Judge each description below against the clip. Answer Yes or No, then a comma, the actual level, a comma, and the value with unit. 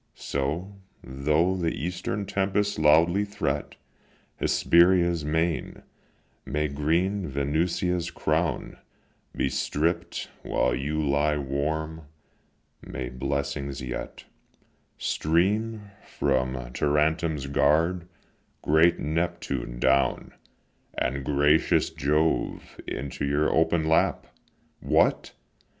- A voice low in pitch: Yes, very low, 75 Hz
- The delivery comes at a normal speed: No, slow, 85 wpm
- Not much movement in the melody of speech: No, average, 3.4 semitones